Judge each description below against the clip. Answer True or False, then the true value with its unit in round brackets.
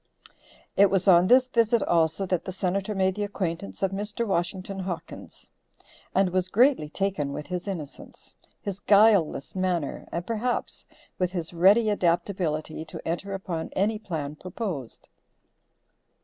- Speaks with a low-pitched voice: False (185 Hz)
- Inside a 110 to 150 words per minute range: True (140 wpm)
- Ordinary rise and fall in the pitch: True (3.1 semitones)